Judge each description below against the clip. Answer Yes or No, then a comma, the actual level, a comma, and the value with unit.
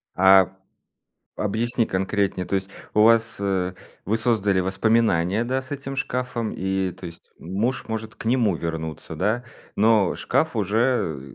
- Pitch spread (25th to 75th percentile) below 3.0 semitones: No, average, 3.7 semitones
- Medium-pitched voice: No, low, 105 Hz